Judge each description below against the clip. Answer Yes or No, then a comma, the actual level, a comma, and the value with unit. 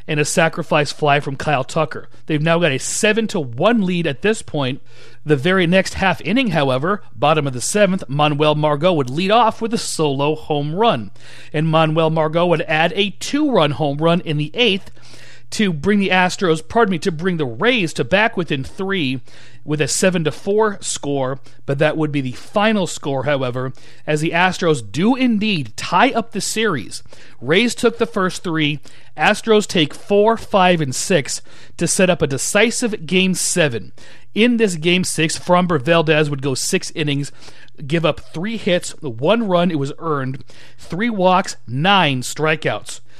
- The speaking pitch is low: No, medium, 165 Hz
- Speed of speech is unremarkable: Yes, average, 180 wpm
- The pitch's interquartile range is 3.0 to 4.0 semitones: No, average, 5.1 semitones